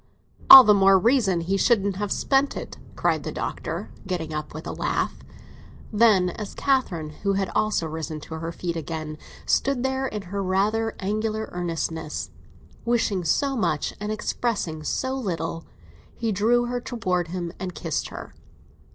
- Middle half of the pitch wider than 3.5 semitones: Yes, average, 5.2 semitones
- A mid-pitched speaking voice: No, high, 195 Hz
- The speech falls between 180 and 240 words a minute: No, average, 160 wpm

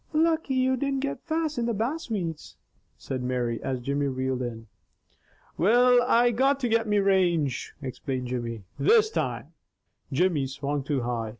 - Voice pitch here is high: No, medium, 180 Hz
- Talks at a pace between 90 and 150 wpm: No, average, 165 wpm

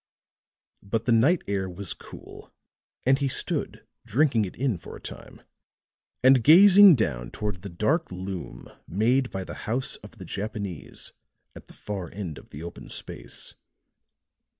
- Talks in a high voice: No, low, 105 Hz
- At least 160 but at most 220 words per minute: No, average, 150 wpm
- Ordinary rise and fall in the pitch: No, wide, 6.2 semitones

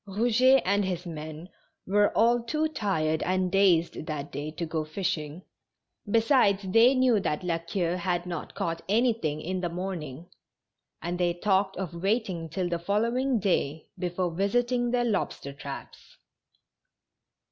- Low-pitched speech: No, medium, 185 Hz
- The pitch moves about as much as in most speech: Yes, average, 4.5 semitones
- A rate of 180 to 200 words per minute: No, average, 145 wpm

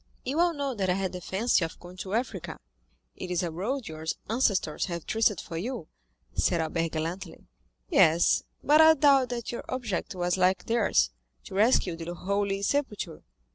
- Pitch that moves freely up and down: Yes, wide, 5.8 semitones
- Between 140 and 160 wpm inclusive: No, average, 175 wpm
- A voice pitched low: No, high, 190 Hz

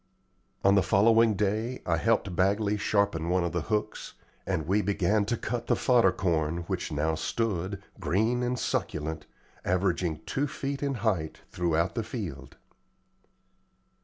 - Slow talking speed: No, average, 145 wpm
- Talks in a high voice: No, low, 100 Hz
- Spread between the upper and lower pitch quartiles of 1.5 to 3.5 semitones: No, average, 4.6 semitones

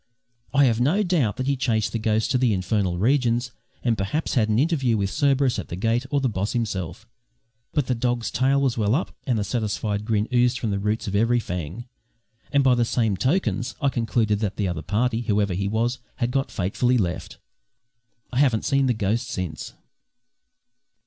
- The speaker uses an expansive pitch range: No, average, 3.8 semitones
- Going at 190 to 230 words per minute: Yes, average, 195 wpm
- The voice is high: No, low, 115 Hz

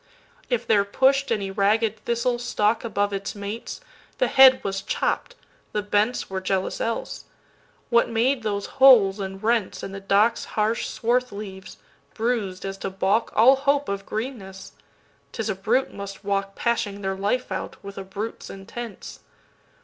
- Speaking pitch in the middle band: No, high, 210 Hz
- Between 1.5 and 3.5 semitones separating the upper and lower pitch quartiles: Yes, average, 3.2 semitones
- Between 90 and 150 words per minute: Yes, average, 140 wpm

